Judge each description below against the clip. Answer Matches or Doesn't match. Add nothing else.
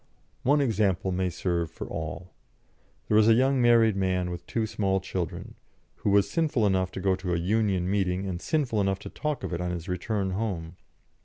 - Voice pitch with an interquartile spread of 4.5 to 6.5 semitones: Doesn't match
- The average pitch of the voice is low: Matches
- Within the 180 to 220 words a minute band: Matches